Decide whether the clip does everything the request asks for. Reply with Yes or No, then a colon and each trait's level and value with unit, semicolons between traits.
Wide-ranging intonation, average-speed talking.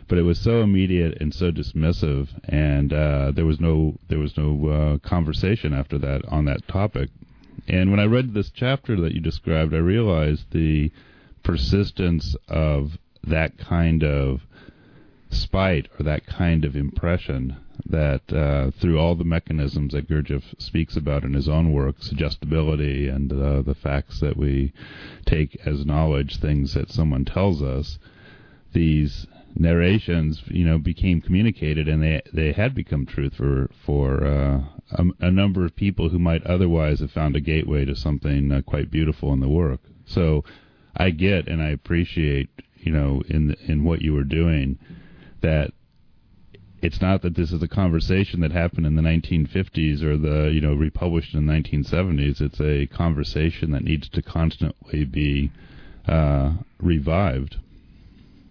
No: average, 3.0 semitones; average, 160 wpm